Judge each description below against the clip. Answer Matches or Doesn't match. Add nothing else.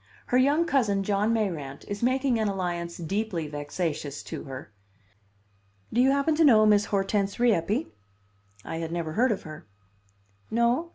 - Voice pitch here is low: Doesn't match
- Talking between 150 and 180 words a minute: Matches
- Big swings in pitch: Matches